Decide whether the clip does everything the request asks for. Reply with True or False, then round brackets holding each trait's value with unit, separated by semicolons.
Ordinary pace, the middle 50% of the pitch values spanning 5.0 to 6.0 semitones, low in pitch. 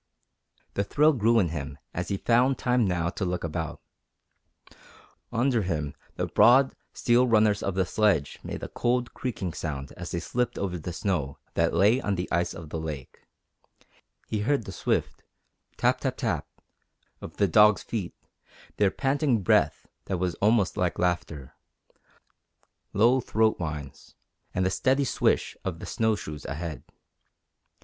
True (155 wpm; 5.5 semitones; 95 Hz)